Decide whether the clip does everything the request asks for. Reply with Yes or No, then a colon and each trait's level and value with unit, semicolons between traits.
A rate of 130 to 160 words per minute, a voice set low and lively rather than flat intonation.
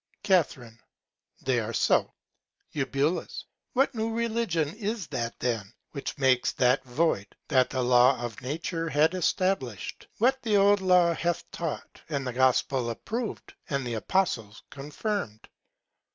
No: slow, 135 wpm; medium, 150 Hz; wide, 7.3 semitones